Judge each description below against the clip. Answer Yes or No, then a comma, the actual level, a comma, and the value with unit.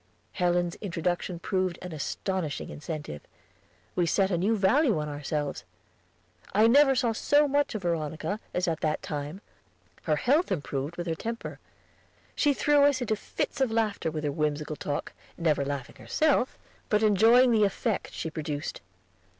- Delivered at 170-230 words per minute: No, average, 155 wpm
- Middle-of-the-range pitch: Yes, medium, 180 Hz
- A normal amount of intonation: No, wide, 6.6 semitones